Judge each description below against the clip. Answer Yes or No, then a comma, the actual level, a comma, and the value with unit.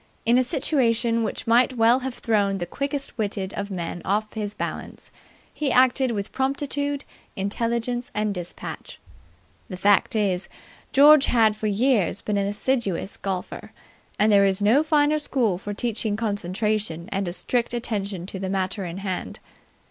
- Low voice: No, high, 215 Hz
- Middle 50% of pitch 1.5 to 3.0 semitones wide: No, average, 3.9 semitones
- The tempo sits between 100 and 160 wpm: Yes, average, 155 wpm